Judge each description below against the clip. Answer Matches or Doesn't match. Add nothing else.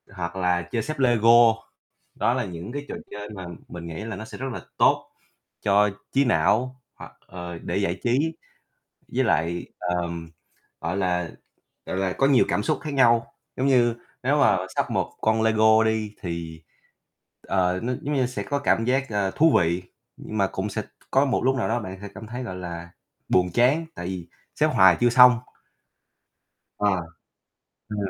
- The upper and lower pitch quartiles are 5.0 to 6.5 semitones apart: Matches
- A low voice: Matches